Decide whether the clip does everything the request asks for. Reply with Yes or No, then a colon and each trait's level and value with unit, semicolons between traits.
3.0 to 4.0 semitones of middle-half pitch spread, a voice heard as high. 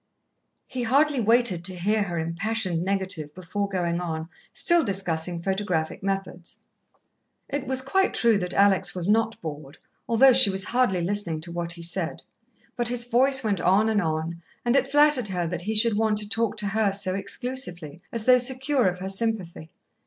No: average, 5.1 semitones; high, 200 Hz